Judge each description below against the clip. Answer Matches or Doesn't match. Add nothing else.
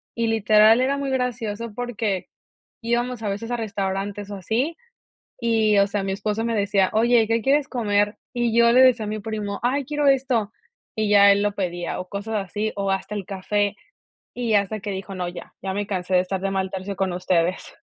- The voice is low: Doesn't match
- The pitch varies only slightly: Doesn't match